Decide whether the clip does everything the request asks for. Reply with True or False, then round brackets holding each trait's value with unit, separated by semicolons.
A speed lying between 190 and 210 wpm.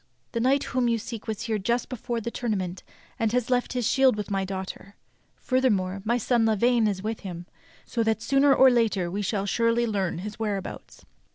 True (195 wpm)